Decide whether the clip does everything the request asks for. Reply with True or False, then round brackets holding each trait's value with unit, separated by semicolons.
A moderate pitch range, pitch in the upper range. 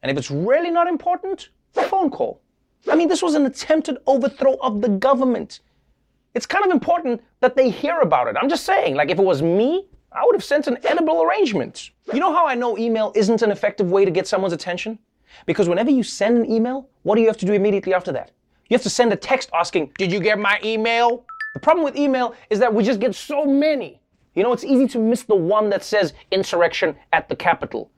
False (5.8 semitones; 245 Hz)